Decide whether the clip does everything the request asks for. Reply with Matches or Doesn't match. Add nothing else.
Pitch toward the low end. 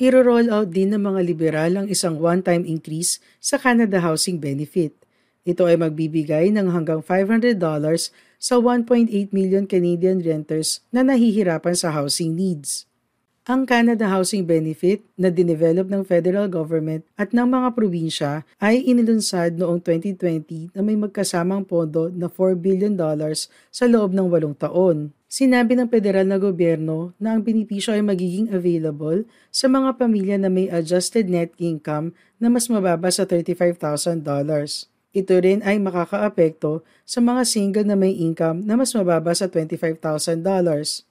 Doesn't match